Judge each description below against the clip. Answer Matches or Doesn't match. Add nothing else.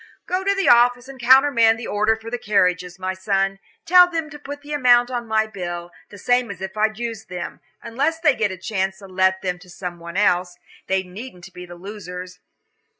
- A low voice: Doesn't match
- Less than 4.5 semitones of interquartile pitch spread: Doesn't match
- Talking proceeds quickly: Matches